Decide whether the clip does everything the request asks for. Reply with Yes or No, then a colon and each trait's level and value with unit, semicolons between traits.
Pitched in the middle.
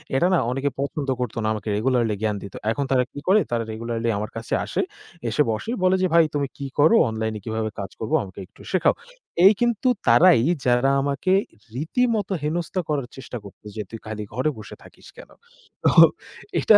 No: low, 125 Hz